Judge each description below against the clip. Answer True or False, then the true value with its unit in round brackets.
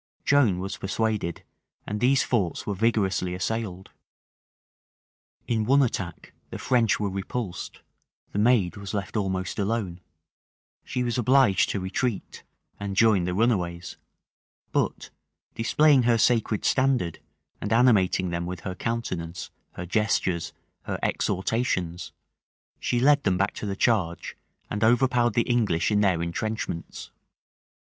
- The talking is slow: True (130 wpm)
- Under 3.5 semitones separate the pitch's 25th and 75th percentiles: False (4.3 semitones)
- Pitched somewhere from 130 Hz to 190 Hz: False (105 Hz)